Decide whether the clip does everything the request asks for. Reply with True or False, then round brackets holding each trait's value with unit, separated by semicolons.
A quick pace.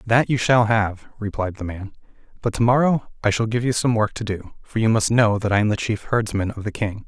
True (265 wpm)